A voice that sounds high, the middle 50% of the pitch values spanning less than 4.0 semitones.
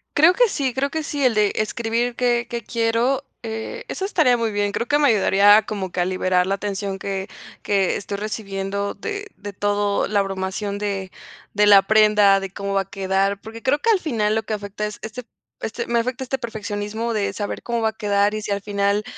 Yes: high, 210 Hz; average, 2.8 semitones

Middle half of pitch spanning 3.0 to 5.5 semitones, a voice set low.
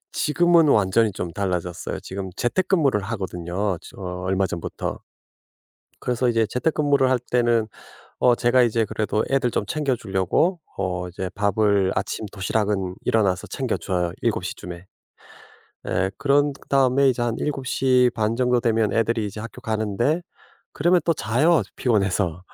Yes: average, 5.1 semitones; low, 110 Hz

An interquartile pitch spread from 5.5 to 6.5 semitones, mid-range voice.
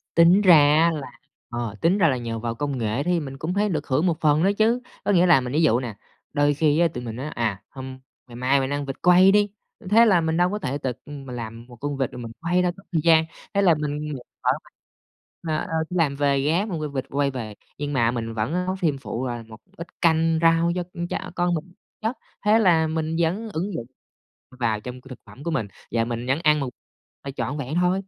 No: average, 5.1 semitones; medium, 150 Hz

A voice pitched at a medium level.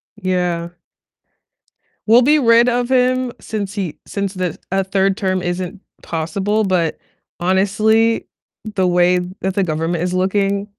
No: high, 195 Hz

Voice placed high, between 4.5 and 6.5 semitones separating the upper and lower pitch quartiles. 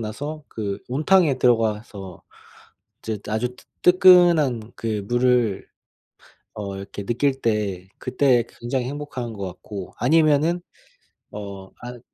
No: low, 120 Hz; average, 5.3 semitones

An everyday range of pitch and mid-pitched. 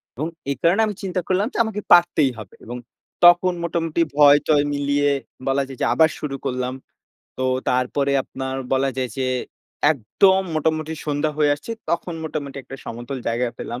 Yes: average, 4.1 semitones; medium, 145 Hz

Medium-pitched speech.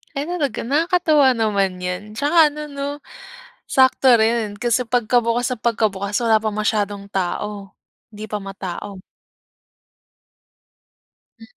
No: high, 220 Hz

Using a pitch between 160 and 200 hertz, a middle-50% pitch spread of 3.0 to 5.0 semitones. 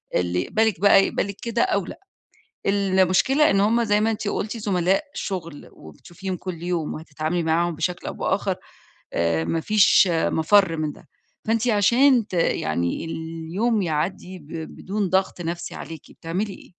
Yes: medium, 185 Hz; average, 4.1 semitones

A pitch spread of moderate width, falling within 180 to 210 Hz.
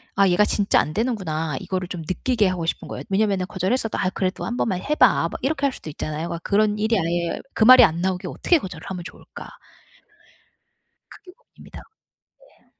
Yes: average, 4.3 semitones; high, 190 Hz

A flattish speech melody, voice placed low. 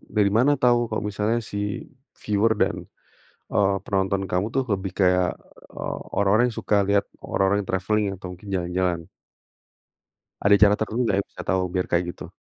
Yes: narrow, 2.3 semitones; low, 100 Hz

